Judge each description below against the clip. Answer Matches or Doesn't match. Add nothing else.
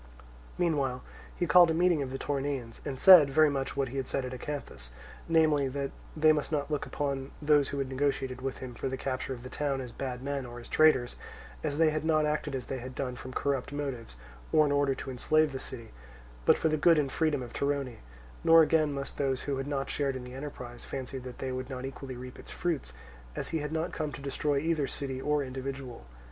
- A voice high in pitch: Doesn't match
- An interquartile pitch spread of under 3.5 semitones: Matches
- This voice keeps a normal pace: Doesn't match